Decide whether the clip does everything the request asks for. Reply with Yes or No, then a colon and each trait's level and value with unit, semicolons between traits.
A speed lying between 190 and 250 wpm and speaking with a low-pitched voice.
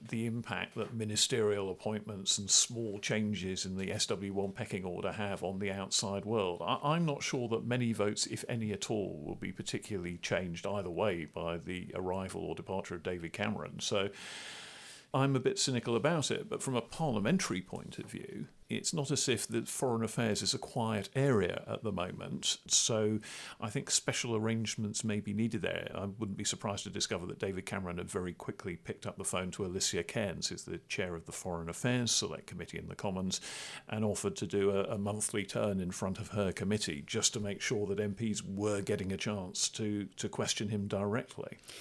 Yes: average, 200 wpm; low, 105 Hz